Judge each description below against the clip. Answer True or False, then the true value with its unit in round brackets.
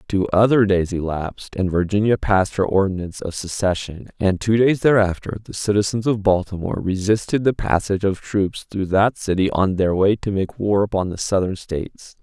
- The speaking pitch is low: True (100 Hz)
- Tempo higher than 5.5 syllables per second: False (5.4 syllables/s)